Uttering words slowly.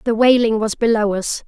No: fast, 205 wpm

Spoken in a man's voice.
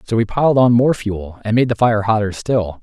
Yes: male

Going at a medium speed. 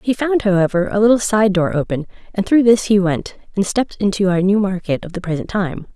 No: fast, 230 wpm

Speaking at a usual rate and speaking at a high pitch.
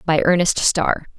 No: average, 150 wpm; medium, 170 Hz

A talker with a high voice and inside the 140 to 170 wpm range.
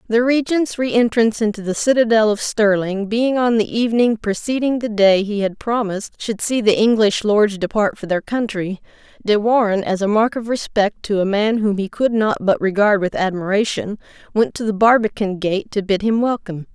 No: high, 215 Hz; average, 195 wpm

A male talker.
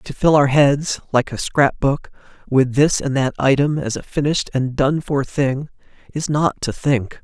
Yes: male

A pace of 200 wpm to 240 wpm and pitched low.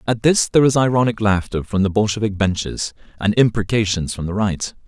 No: average, 185 wpm; low, 105 Hz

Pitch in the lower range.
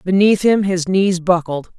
No: medium, 185 Hz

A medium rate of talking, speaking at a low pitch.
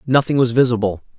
Yes: average, 150 wpm; low, 120 Hz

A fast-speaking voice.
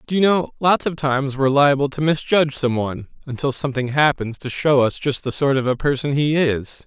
Yes: fast, 225 wpm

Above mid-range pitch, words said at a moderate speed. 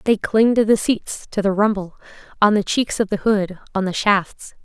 No: high, 205 Hz; fast, 220 wpm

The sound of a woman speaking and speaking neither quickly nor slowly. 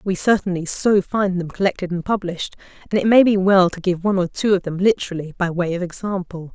No: female; fast, 230 wpm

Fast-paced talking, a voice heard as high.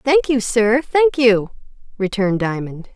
No: average, 140 wpm; high, 230 Hz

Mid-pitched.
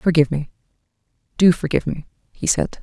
Yes: medium, 150 Hz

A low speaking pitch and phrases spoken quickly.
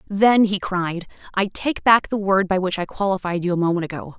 No: high, 190 Hz; fast, 230 wpm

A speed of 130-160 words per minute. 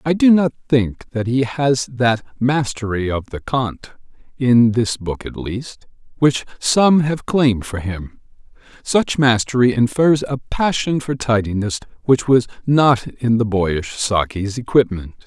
Yes: average, 140 wpm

